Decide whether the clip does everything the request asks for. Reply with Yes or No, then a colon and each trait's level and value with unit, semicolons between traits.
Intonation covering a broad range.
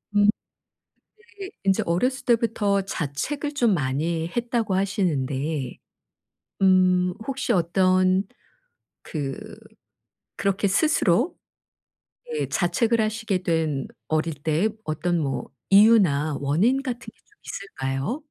Yes: wide, 6.3 semitones